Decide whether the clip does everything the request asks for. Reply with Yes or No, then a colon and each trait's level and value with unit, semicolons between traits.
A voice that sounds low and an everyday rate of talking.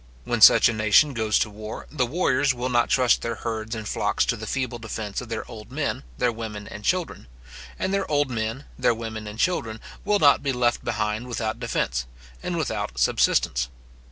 Yes: low, 115 Hz; average, 195 wpm